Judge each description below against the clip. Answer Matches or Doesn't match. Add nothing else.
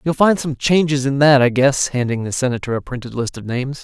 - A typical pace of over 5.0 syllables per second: Matches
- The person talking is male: Matches